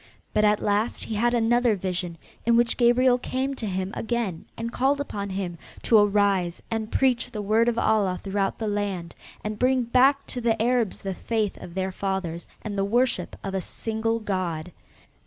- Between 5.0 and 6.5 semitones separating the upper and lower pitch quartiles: No, average, 3.6 semitones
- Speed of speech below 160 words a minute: No, average, 185 wpm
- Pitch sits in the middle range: No, high, 215 Hz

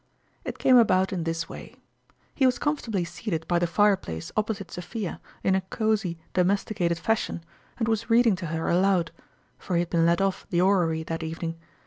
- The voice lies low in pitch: No, medium, 185 Hz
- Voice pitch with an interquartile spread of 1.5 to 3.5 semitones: No, average, 4.1 semitones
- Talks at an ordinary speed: Yes, average, 190 wpm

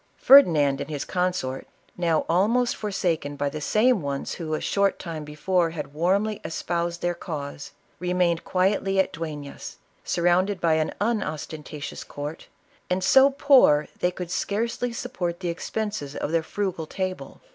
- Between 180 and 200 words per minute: No, average, 150 wpm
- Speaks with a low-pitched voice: No, medium, 175 Hz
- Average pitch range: Yes, average, 4.0 semitones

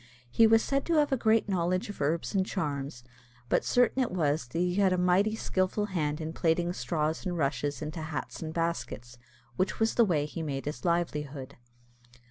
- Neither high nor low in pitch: Yes, medium, 170 Hz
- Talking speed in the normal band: Yes, average, 195 wpm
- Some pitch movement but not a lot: Yes, average, 4.8 semitones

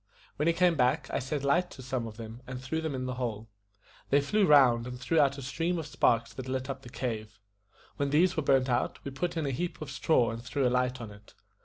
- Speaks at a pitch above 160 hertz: No, low, 130 Hz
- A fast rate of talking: Yes, fast, 260 wpm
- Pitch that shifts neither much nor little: Yes, average, 3.3 semitones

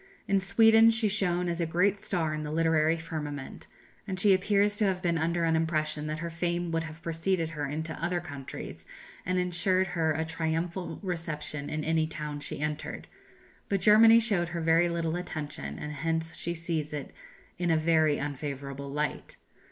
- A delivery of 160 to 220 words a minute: Yes, average, 180 wpm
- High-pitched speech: No, medium, 165 Hz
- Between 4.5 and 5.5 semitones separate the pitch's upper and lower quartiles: No, average, 2.7 semitones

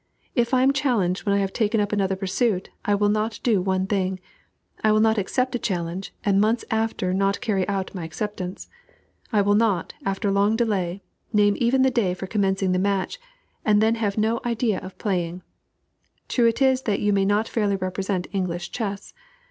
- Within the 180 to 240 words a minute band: Yes, average, 195 wpm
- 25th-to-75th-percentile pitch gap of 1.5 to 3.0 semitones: Yes, average, 2.7 semitones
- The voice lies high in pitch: Yes, high, 205 Hz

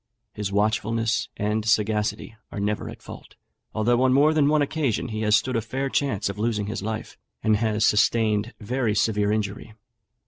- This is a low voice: Yes, low, 110 Hz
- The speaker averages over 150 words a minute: Yes, average, 175 wpm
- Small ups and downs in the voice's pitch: Yes, narrow, 2.1 semitones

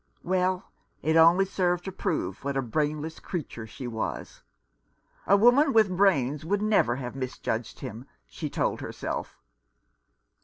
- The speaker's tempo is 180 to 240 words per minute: No, average, 145 wpm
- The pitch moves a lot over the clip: Yes, wide, 6.5 semitones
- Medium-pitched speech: Yes, medium, 165 Hz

